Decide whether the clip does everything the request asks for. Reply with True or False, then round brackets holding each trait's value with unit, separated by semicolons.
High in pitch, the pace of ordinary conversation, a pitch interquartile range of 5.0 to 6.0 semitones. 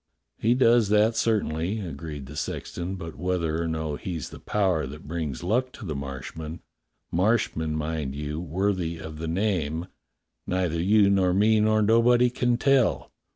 False (90 Hz; 170 wpm; 5.4 semitones)